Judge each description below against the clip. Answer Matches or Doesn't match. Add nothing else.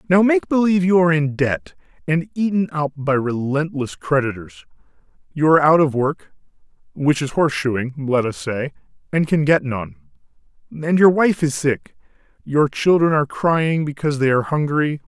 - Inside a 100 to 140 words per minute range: Doesn't match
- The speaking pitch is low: Doesn't match